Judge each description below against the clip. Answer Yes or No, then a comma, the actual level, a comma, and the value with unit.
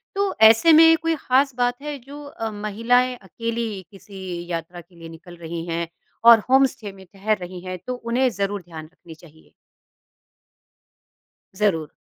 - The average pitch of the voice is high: Yes, high, 210 Hz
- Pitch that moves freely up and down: Yes, wide, 6.2 semitones